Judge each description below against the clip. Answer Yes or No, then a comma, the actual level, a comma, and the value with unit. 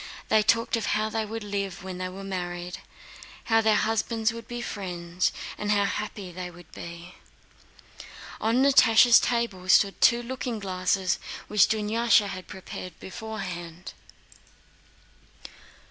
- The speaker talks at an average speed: No, slow, 130 wpm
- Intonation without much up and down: No, average, 3.5 semitones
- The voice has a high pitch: Yes, high, 205 Hz